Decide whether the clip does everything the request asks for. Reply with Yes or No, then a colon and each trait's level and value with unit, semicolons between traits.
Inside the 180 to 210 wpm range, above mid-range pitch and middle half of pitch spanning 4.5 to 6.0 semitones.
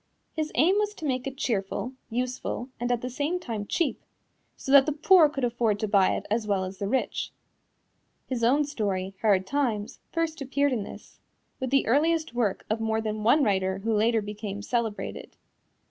Yes: average, 190 wpm; high, 240 Hz; average, 5.1 semitones